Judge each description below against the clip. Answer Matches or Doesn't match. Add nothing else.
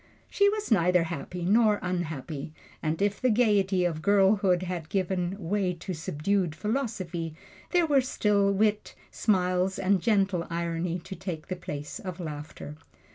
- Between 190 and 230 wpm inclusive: Doesn't match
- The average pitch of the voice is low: Doesn't match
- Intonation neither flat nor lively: Matches